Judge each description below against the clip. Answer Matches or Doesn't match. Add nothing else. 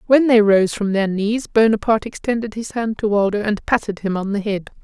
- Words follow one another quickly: Matches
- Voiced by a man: Doesn't match